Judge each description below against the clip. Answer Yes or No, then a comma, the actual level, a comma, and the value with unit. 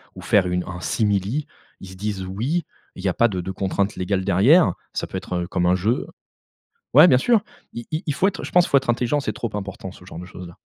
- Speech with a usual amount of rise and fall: No, wide, 6.2 semitones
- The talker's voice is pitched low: Yes, low, 100 Hz